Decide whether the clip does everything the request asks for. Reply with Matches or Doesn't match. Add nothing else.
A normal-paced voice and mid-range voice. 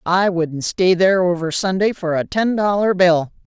Matches